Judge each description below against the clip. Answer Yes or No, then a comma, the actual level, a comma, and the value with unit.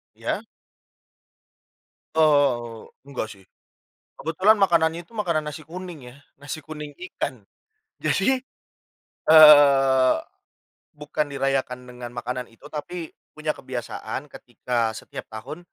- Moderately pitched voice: Yes, medium, 145 Hz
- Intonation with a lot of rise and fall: No, average, 4.0 semitones